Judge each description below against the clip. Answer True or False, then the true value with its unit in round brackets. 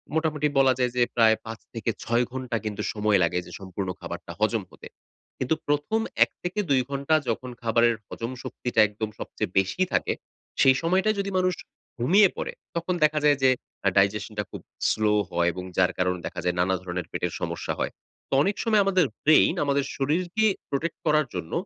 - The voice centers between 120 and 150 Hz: True (130 Hz)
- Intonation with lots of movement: True (7.1 semitones)